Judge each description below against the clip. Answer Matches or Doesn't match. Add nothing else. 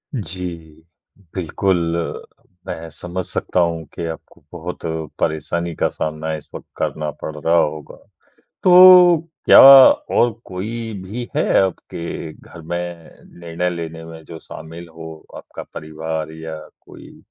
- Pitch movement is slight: Matches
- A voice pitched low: Matches